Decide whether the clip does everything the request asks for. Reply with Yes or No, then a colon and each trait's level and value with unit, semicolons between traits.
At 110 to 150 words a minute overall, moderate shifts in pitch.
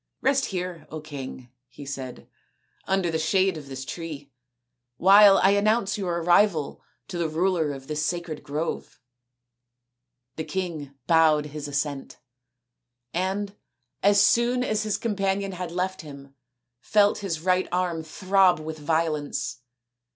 Yes: slow, 135 wpm; average, 4.2 semitones